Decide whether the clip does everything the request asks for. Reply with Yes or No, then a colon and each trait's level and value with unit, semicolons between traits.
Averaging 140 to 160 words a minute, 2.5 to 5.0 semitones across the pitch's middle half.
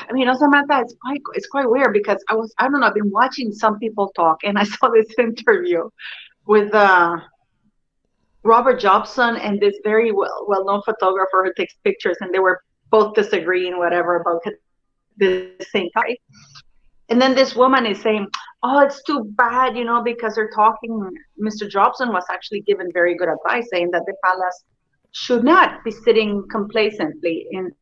No: average, 175 wpm; average, 4.5 semitones